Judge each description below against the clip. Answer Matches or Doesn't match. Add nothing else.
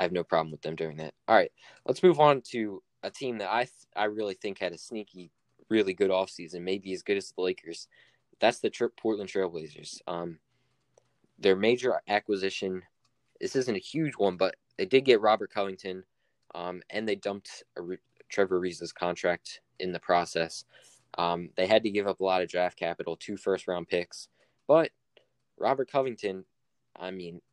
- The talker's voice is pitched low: Matches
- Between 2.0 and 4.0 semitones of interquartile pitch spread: Matches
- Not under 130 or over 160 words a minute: Doesn't match